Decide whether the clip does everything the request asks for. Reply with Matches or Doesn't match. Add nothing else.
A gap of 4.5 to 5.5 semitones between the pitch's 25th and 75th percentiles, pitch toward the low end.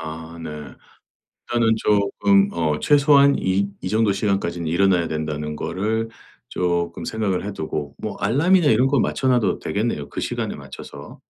Matches